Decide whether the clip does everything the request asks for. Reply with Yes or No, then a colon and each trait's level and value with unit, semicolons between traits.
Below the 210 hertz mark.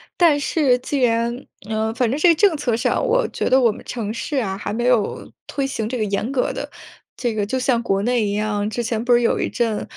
No: high, 240 Hz